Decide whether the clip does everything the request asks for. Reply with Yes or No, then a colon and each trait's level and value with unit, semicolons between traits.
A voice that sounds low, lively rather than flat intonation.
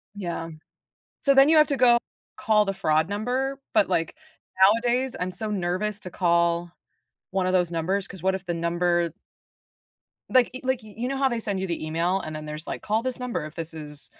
No: high, 190 Hz; wide, 5.9 semitones